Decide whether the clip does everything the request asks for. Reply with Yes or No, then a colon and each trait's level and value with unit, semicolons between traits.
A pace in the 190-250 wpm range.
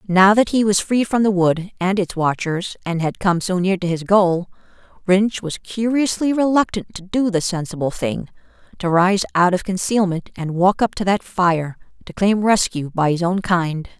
Yes: average, 195 wpm